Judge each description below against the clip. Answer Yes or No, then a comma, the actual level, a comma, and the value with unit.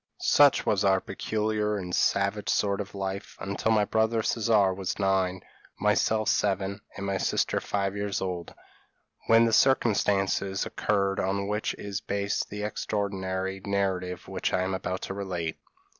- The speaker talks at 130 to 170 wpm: Yes, average, 155 wpm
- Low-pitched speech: Yes, low, 100 Hz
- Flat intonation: Yes, narrow, 1.6 semitones